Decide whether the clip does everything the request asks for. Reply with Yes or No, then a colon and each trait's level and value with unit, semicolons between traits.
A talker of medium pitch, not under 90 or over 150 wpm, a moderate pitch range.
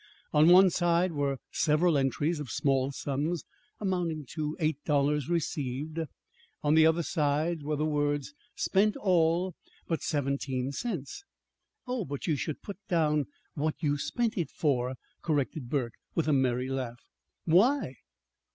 Yes: medium, 150 Hz; average, 145 wpm; average, 3.3 semitones